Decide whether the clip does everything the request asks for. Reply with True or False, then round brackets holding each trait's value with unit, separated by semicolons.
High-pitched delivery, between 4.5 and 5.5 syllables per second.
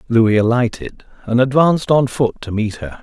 False (120 Hz; 5.4 syllables/s)